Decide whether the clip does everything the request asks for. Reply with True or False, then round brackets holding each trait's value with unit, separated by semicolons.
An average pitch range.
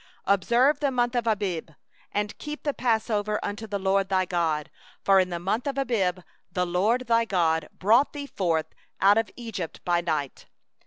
True (4.7 semitones)